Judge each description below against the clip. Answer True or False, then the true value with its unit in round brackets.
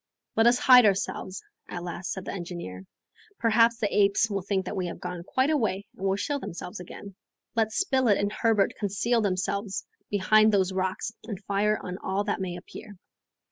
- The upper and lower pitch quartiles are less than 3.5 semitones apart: True (2.7 semitones)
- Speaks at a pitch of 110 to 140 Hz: False (200 Hz)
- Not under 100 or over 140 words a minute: False (180 wpm)